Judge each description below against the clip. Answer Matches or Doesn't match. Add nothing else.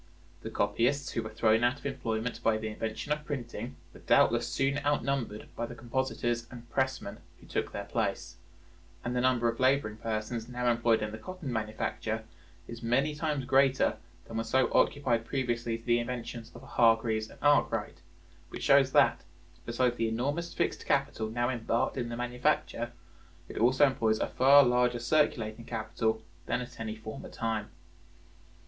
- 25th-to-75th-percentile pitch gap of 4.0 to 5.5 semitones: Doesn't match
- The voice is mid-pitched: Doesn't match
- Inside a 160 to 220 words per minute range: Matches